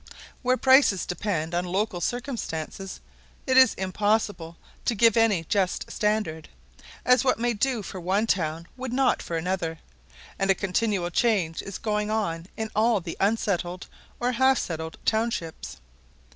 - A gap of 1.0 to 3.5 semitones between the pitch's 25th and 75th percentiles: No, average, 4.7 semitones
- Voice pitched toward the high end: Yes, high, 205 Hz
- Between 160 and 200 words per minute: No, average, 145 wpm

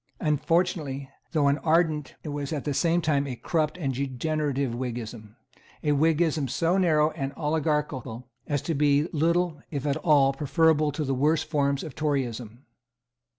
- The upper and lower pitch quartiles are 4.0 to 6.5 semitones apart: No, narrow, 2.6 semitones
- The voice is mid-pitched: Yes, medium, 150 Hz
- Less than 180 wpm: Yes, average, 155 wpm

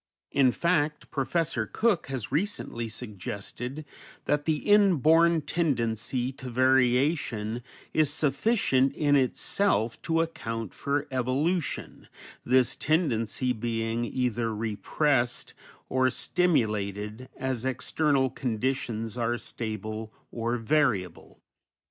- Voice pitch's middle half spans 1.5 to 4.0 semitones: No, average, 4.7 semitones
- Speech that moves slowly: Yes, slow, 95 wpm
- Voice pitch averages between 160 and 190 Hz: No, low, 130 Hz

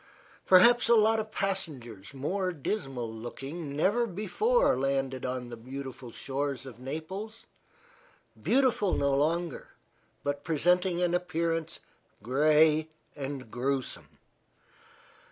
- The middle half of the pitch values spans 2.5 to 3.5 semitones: No, wide, 5.6 semitones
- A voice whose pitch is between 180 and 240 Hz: No, medium, 155 Hz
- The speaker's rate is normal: No, slow, 105 wpm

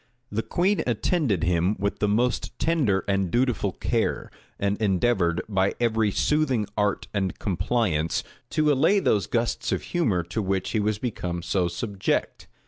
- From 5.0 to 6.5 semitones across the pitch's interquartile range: No, average, 4.3 semitones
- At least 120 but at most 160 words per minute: Yes, average, 150 wpm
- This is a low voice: Yes, low, 105 Hz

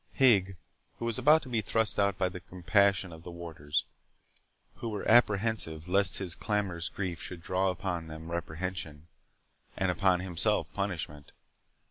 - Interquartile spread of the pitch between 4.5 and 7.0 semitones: No, average, 3.0 semitones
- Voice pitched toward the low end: Yes, very low, 95 Hz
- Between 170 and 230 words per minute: No, average, 145 wpm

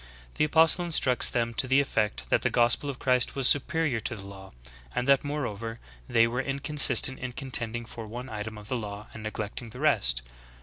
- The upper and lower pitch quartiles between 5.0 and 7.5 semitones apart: No, average, 4.1 semitones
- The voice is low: Yes, low, 120 Hz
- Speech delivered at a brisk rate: Yes, fast, 210 wpm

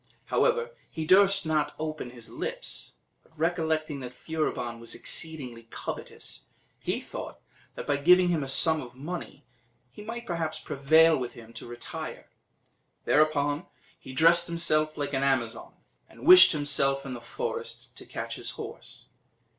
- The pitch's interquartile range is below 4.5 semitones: Yes, average, 4.0 semitones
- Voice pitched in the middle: Yes, medium, 155 Hz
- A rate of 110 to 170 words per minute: Yes, average, 155 wpm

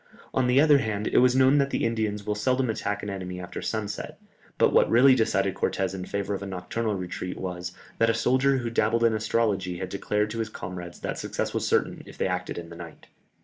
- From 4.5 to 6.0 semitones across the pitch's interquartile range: No, average, 3.7 semitones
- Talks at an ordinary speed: No, fast, 230 wpm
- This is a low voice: Yes, low, 105 Hz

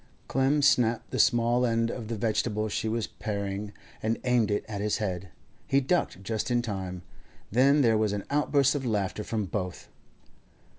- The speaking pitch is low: Yes, low, 110 Hz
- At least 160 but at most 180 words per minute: Yes, average, 170 wpm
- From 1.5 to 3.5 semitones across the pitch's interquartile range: Yes, average, 3.2 semitones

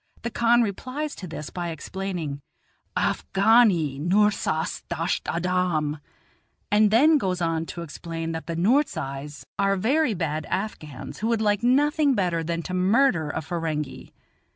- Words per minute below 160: Yes, average, 140 wpm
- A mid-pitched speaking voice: Yes, medium, 180 Hz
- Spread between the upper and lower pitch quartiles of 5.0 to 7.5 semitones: Yes, average, 5.3 semitones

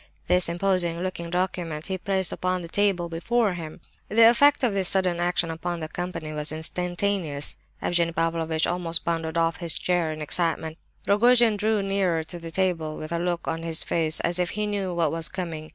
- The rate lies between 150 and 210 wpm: Yes, average, 190 wpm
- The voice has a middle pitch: Yes, medium, 175 Hz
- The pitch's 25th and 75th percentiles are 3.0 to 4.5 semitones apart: No, narrow, 2.4 semitones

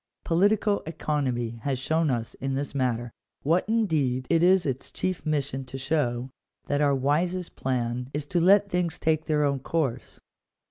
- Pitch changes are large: No, average, 4.4 semitones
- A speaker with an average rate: Yes, average, 175 wpm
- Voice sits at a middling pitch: Yes, medium, 145 Hz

